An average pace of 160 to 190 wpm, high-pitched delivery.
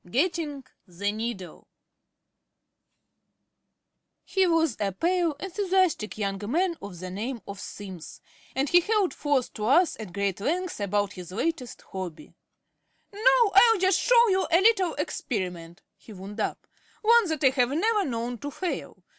No: average, 145 wpm; very high, 275 Hz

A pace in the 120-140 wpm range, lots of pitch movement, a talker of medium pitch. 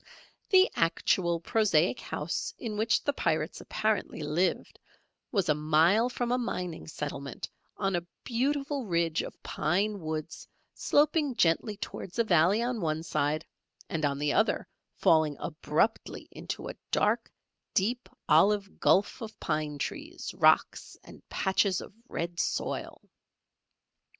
Yes: slow, 135 wpm; wide, 6.1 semitones; medium, 180 Hz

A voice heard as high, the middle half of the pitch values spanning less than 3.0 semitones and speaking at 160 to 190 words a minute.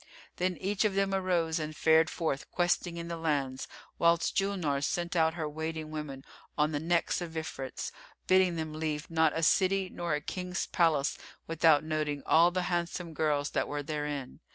No: medium, 160 Hz; narrow, 2.5 semitones; average, 175 wpm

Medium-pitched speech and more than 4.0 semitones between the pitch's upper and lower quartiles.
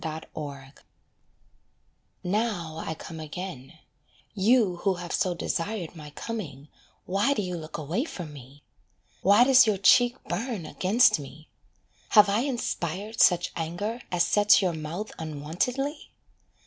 Yes: medium, 180 Hz; wide, 5.4 semitones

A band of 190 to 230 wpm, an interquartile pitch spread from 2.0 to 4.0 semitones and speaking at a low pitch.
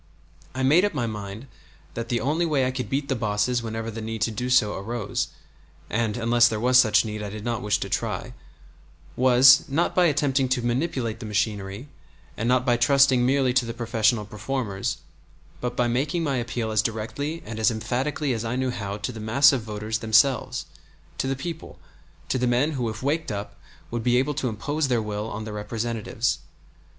Yes: average, 200 wpm; average, 3.3 semitones; low, 120 Hz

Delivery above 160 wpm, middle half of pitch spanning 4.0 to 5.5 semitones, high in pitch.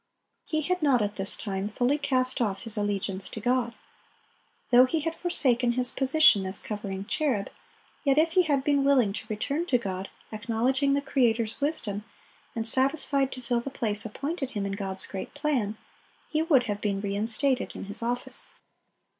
Yes: average, 180 wpm; average, 5.1 semitones; high, 245 Hz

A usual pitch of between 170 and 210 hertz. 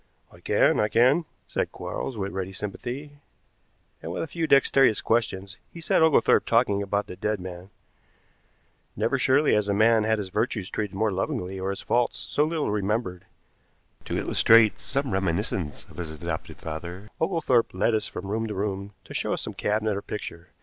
No: low, 105 Hz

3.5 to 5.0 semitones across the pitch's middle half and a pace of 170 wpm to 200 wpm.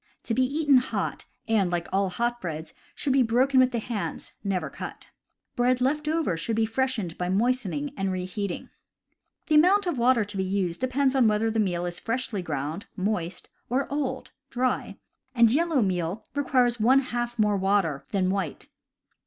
No: wide, 5.4 semitones; average, 175 wpm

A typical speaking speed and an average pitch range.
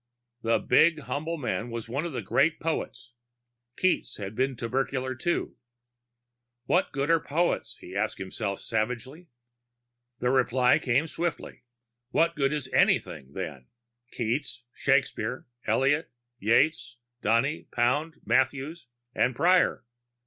No: slow, 125 wpm; average, 4.6 semitones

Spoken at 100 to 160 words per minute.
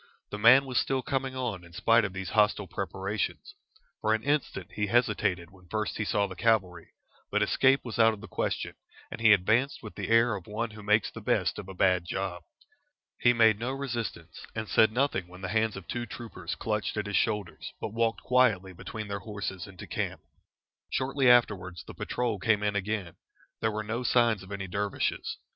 No: average, 200 wpm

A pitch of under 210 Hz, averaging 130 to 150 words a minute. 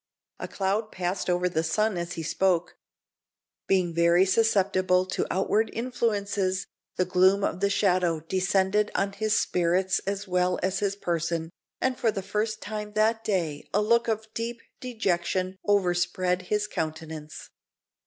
Yes: high, 190 Hz; average, 145 wpm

